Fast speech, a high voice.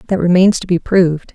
No: fast, 225 wpm; medium, 175 Hz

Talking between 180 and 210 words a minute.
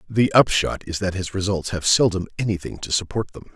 Yes: average, 200 wpm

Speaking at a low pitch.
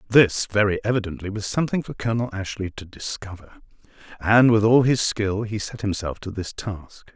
Yes: low, 105 Hz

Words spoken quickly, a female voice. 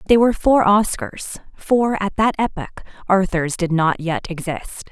No: average, 160 wpm; female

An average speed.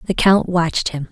No: fast, 215 wpm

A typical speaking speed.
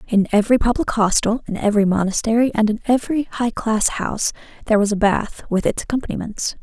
Yes: average, 180 wpm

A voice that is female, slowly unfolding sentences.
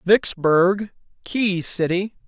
No: male; slow, 80 wpm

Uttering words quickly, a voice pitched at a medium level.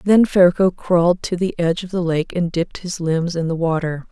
Yes: fast, 235 wpm; medium, 175 Hz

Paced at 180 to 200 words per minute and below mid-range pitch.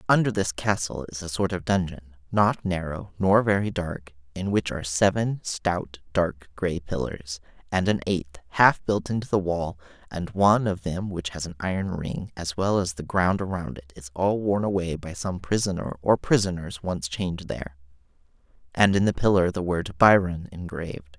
Yes: average, 185 wpm; very low, 90 Hz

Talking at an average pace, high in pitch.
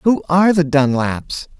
No: average, 150 wpm; medium, 155 Hz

